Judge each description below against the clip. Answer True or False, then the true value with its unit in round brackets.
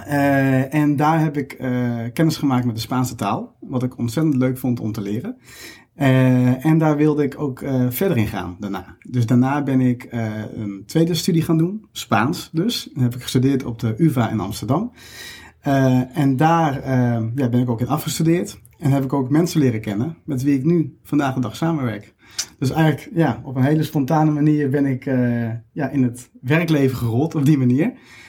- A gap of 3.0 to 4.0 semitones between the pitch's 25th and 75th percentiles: True (3.7 semitones)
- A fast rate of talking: True (205 wpm)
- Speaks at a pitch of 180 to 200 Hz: False (130 Hz)